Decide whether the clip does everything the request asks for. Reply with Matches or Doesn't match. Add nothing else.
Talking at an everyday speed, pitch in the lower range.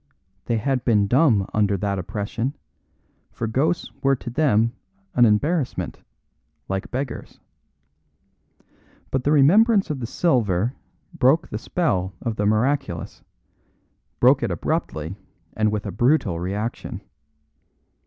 Doesn't match